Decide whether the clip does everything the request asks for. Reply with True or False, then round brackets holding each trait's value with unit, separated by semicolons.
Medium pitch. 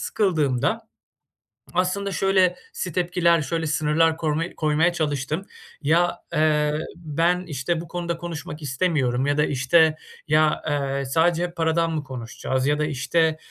True (160 Hz)